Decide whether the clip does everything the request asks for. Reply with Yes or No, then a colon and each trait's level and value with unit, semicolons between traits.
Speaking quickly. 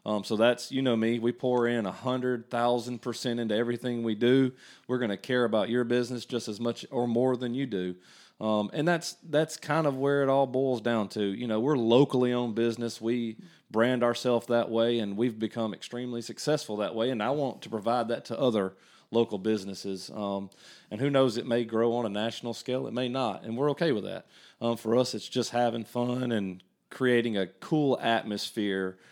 Yes: fast, 210 wpm